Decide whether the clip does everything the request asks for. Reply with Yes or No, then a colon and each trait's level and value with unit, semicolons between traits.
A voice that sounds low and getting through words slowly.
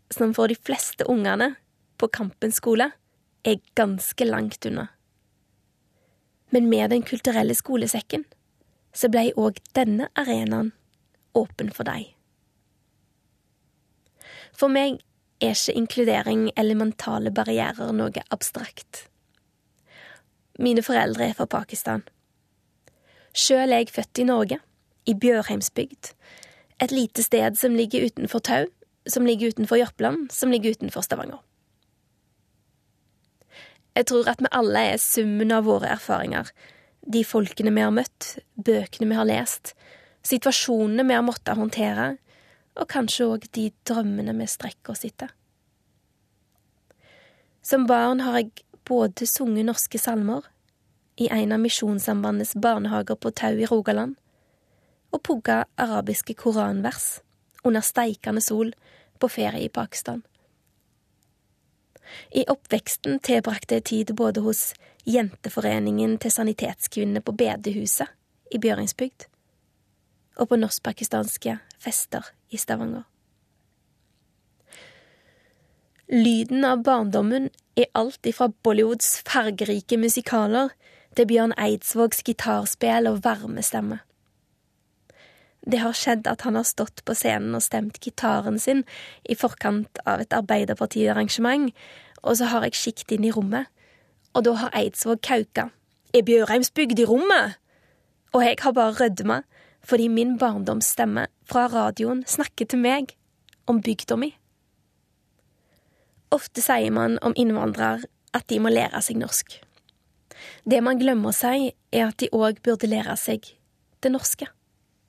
No: high, 230 Hz; slow, 120 wpm